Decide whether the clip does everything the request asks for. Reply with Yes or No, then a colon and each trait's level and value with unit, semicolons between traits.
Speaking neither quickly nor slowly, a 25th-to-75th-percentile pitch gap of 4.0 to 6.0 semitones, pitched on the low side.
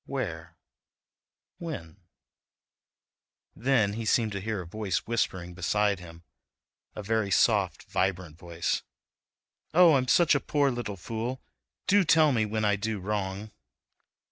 No: slow, 130 wpm; average, 4.8 semitones; low, 105 Hz